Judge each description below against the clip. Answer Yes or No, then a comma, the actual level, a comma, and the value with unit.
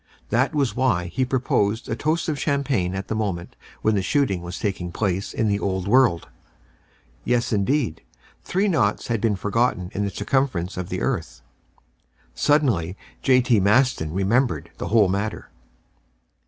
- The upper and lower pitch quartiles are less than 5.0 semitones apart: No, average, 5.3 semitones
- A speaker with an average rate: Yes, average, 155 wpm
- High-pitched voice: No, low, 110 Hz